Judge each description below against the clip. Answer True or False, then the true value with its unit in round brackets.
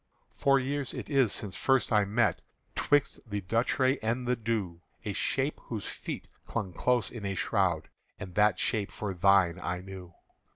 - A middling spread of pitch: True (4.7 semitones)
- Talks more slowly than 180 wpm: True (170 wpm)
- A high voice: False (105 Hz)